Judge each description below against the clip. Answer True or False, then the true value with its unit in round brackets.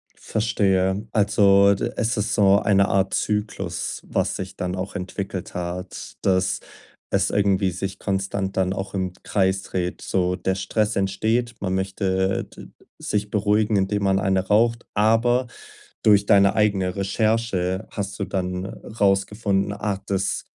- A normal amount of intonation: False (1.7 semitones)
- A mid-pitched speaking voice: False (100 Hz)